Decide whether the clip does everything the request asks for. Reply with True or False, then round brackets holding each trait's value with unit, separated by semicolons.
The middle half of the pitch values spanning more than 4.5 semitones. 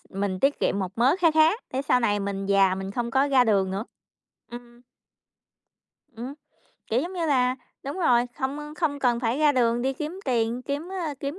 False (4.2 semitones)